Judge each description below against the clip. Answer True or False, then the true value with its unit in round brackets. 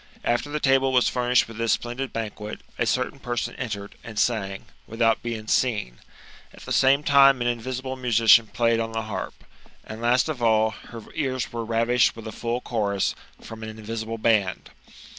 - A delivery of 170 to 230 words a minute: True (180 wpm)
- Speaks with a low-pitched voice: True (115 Hz)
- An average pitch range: False (2.2 semitones)